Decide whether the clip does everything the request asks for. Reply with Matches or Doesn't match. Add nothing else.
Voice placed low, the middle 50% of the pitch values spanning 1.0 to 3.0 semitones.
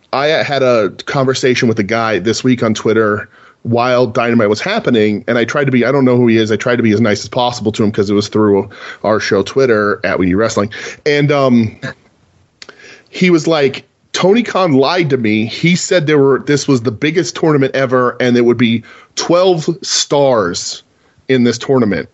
Doesn't match